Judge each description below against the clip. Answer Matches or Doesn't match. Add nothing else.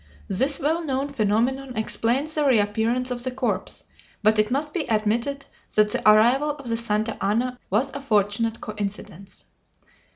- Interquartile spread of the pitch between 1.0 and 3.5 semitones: Doesn't match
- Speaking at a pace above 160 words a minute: Doesn't match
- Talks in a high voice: Matches